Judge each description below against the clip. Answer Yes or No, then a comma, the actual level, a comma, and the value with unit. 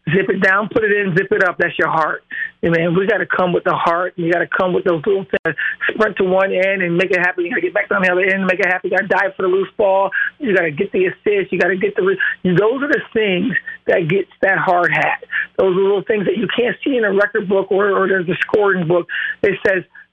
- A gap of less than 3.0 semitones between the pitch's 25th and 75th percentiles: No, average, 4.5 semitones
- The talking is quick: Yes, fast, 300 wpm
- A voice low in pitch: No, high, 195 Hz